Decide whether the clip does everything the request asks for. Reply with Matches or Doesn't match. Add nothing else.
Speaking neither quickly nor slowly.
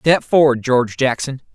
Matches